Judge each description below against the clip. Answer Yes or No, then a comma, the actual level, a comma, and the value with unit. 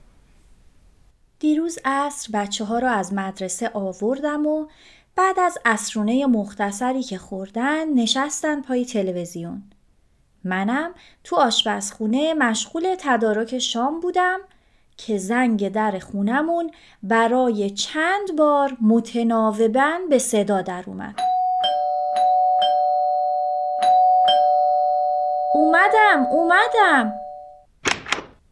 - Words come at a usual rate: No, slow, 80 wpm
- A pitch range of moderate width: No, wide, 7.5 semitones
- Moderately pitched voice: No, high, 230 Hz